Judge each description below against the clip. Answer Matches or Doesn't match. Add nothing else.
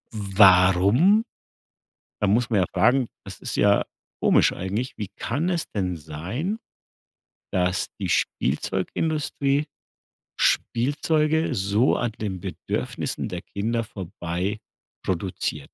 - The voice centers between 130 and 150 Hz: Doesn't match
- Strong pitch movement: Matches